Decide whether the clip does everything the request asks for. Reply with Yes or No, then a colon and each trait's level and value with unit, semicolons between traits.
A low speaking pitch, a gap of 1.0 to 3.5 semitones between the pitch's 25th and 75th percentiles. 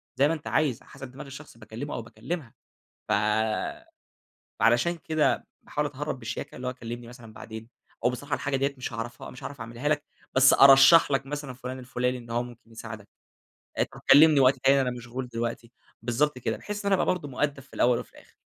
Yes: low, 130 Hz; average, 3.2 semitones